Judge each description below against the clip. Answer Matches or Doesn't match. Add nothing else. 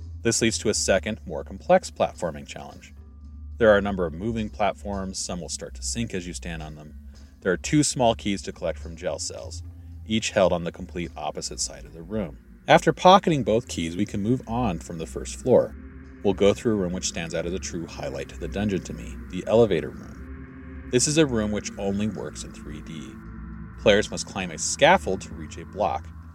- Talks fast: Matches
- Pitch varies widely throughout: Matches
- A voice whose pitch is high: Doesn't match